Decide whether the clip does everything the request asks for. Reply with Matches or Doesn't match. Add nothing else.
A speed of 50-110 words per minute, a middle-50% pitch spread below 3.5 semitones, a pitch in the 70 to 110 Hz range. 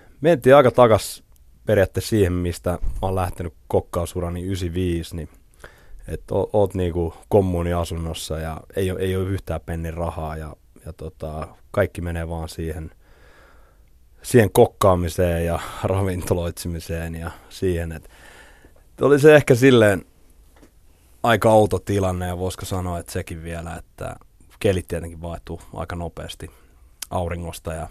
Doesn't match